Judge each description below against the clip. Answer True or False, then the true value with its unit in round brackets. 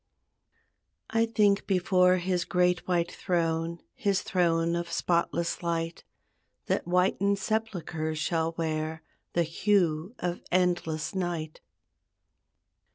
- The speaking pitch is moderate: True (175 Hz)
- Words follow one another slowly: True (100 wpm)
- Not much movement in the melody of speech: True (2.0 semitones)